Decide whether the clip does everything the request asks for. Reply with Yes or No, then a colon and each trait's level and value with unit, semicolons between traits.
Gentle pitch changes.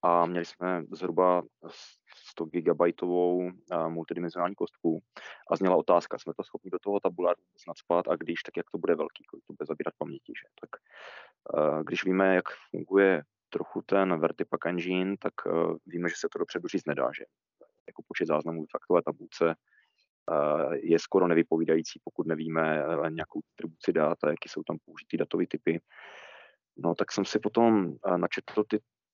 No: average, 3.3 semitones